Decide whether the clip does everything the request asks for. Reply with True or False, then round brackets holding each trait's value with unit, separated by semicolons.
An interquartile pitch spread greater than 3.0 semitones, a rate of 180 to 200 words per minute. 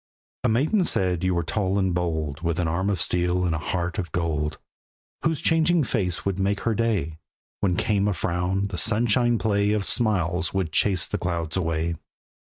True (3.6 semitones; 190 wpm)